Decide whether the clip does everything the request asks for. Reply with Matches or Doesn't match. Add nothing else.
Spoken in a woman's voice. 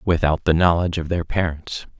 Doesn't match